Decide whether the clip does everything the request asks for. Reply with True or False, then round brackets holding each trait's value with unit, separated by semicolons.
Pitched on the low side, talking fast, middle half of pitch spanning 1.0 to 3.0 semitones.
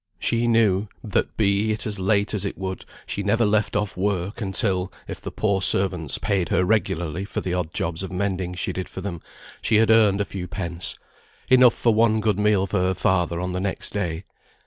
True (100 Hz; 215 wpm; 2.6 semitones)